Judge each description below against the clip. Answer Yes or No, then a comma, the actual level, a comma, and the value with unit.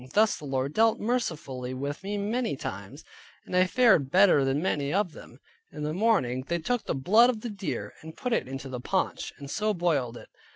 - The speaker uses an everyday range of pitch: No, wide, 7.9 semitones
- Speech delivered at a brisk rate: Yes, fast, 210 wpm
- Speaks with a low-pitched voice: No, medium, 170 Hz